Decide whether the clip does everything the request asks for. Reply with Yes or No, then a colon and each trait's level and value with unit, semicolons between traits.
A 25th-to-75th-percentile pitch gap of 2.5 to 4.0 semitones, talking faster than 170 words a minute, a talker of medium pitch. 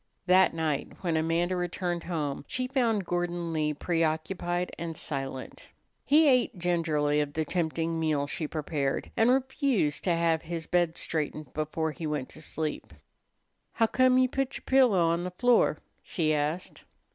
No: average, 3.1 semitones; average, 155 wpm; medium, 170 Hz